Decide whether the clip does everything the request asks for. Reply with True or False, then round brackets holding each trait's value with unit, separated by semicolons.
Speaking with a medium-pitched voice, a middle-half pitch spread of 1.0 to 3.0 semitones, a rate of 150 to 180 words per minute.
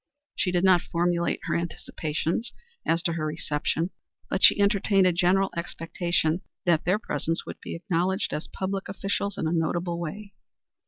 True (175 Hz; 2.5 semitones; 160 wpm)